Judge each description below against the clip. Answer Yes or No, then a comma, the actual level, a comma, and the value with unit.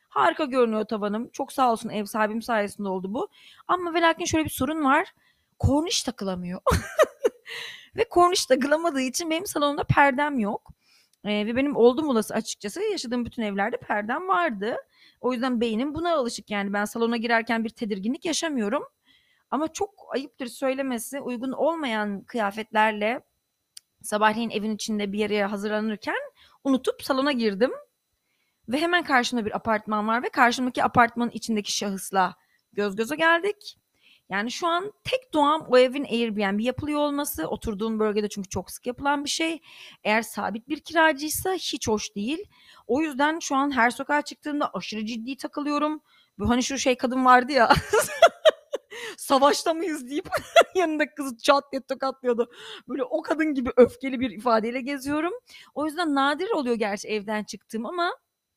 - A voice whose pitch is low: No, very high, 260 Hz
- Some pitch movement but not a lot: No, wide, 5.8 semitones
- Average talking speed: No, fast, 150 wpm